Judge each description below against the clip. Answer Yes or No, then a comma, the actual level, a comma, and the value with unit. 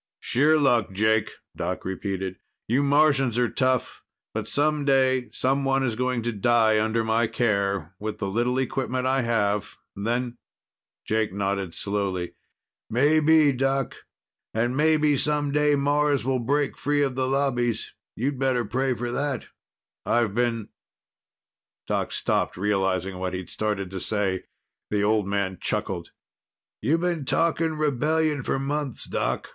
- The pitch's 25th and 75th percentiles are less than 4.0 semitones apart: No, average, 5.0 semitones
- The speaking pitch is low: Yes, low, 125 Hz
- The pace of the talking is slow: No, average, 145 wpm